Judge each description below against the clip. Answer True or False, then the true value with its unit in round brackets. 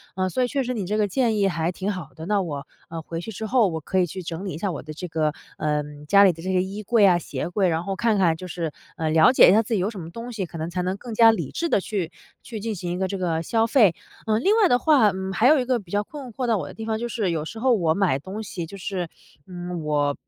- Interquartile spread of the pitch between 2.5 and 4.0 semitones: False (4.6 semitones)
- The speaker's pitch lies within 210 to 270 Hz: False (190 Hz)